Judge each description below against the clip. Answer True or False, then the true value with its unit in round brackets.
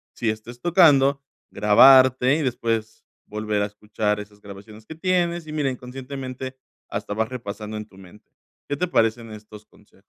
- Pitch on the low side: True (115 Hz)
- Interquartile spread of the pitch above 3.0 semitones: True (4.2 semitones)